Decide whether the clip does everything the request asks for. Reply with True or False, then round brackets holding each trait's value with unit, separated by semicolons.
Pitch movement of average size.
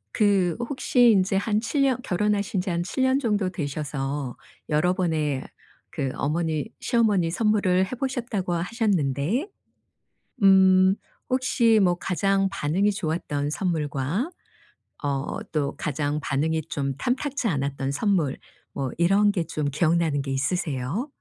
False (6.0 semitones)